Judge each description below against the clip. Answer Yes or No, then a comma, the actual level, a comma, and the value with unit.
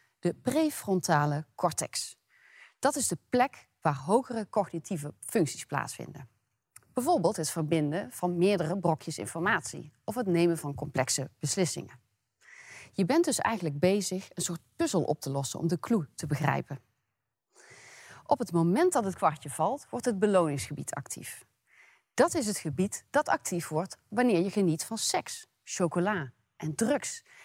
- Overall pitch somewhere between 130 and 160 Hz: No, medium, 175 Hz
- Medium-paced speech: Yes, average, 145 wpm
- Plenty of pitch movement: Yes, wide, 5.7 semitones